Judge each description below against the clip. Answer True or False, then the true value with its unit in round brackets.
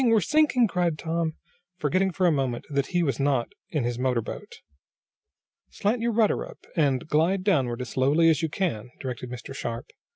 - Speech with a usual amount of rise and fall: False (6.2 semitones)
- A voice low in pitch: False (155 Hz)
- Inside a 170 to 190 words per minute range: True (185 wpm)